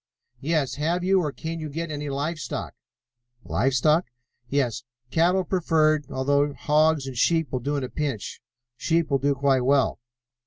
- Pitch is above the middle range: No, medium, 150 Hz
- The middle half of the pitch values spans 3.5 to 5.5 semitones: No, average, 3.0 semitones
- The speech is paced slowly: No, average, 165 wpm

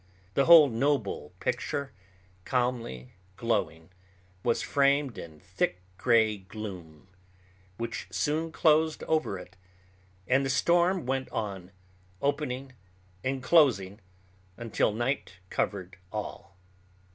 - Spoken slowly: Yes, slow, 100 wpm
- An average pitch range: No, wide, 6.5 semitones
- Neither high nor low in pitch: No, low, 120 Hz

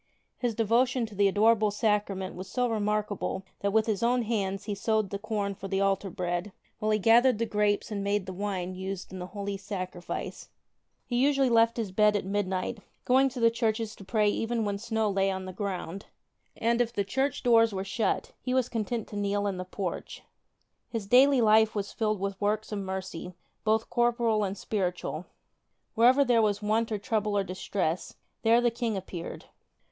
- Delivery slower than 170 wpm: No, average, 195 wpm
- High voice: Yes, high, 210 Hz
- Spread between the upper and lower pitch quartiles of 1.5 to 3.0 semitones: Yes, average, 2.7 semitones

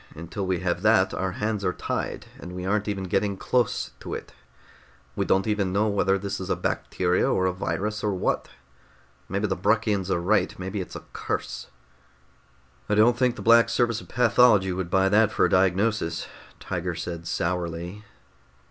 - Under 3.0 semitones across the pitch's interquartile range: Yes, narrow, 2.6 semitones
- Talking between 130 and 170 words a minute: No, average, 180 wpm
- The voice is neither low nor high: No, very low, 95 Hz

